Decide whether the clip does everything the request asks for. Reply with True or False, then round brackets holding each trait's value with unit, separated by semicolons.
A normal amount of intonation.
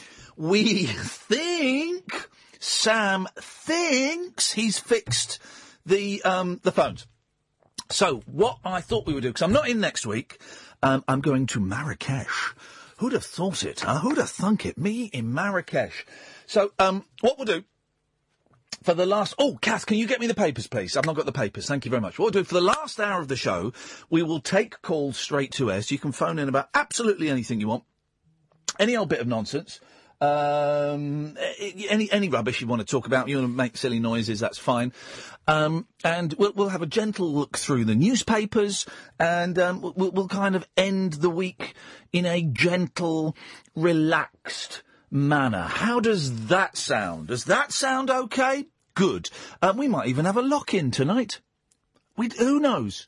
False (7.5 semitones)